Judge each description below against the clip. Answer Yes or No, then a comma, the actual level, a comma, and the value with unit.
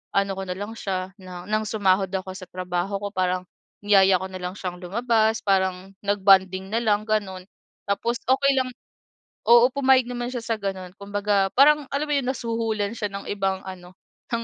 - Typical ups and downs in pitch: Yes, average, 3.4 semitones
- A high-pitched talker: Yes, high, 200 Hz